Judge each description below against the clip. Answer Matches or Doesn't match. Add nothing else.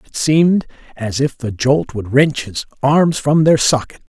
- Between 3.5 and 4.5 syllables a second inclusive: Matches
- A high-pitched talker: Doesn't match